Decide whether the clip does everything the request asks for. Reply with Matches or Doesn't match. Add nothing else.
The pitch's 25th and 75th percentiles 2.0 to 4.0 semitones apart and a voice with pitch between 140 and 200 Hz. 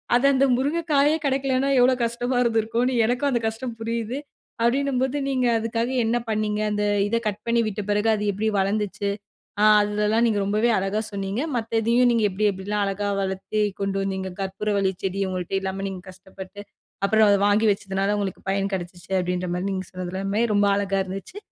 Doesn't match